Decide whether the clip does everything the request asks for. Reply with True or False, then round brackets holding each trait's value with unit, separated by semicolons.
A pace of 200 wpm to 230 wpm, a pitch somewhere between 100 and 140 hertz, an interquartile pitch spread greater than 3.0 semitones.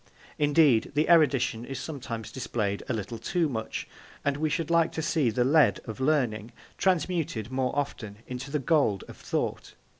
False (170 wpm; 135 Hz; 5.2 semitones)